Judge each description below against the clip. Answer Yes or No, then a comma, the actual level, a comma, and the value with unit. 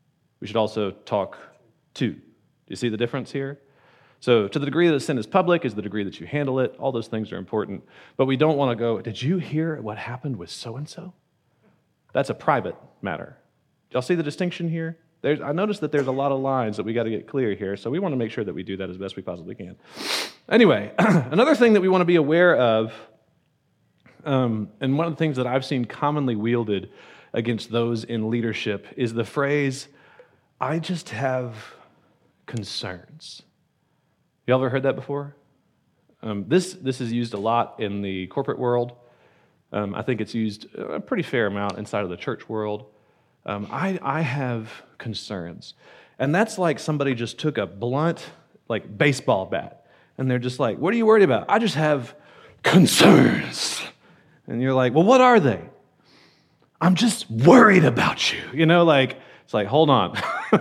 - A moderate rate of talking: Yes, average, 190 wpm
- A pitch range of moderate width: No, wide, 5.9 semitones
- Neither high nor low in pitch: No, low, 130 Hz